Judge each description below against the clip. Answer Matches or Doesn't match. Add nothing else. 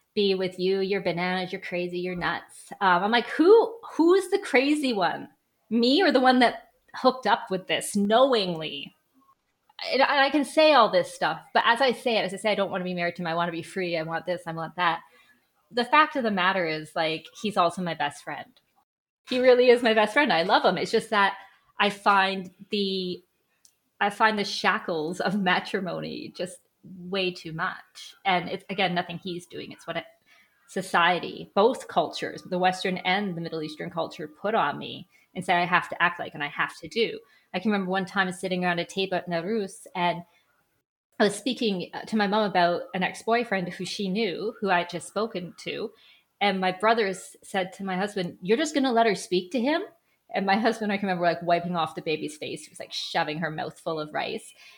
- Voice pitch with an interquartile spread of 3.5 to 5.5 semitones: Matches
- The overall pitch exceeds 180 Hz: Matches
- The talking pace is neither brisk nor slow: Doesn't match